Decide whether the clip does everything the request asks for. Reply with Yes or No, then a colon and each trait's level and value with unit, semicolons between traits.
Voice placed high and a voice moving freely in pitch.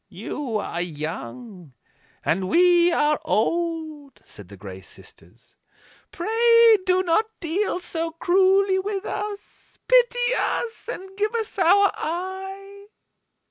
Yes: very high, 360 Hz; wide, 6.5 semitones